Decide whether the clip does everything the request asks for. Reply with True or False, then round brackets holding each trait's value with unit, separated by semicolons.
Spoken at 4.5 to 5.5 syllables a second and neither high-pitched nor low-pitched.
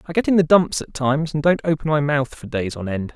False (6.0 syllables/s; 150 Hz)